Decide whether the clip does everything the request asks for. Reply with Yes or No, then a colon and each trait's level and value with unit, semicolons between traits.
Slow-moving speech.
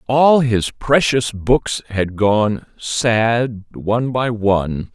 Yes: slow, 120 wpm